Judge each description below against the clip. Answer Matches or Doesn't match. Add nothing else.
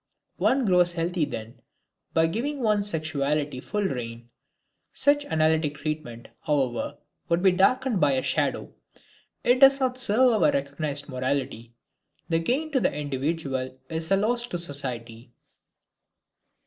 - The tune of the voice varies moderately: Doesn't match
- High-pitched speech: Doesn't match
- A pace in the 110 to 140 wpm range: Matches